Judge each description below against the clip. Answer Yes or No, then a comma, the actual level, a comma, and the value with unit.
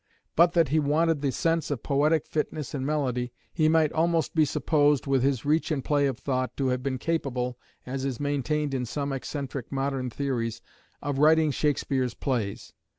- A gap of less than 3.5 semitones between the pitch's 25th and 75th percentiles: Yes, average, 2.8 semitones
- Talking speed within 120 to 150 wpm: No, average, 180 wpm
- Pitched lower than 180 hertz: Yes, medium, 140 Hz